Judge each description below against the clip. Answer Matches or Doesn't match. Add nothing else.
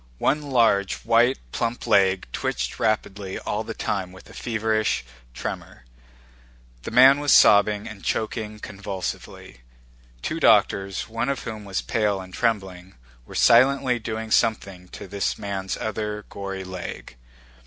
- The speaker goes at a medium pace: Doesn't match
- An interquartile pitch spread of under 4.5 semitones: Matches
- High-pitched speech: Doesn't match